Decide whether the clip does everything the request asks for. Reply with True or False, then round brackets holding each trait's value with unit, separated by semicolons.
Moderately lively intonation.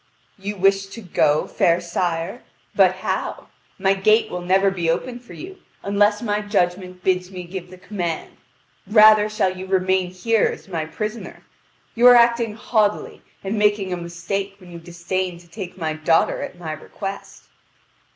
True (3.0 semitones)